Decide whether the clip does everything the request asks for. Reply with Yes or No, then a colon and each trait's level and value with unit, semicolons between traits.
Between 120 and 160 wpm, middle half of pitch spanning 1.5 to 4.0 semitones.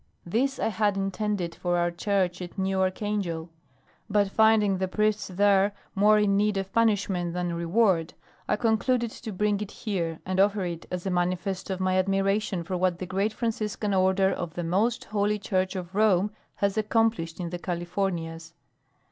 No: average, 175 wpm; average, 2.8 semitones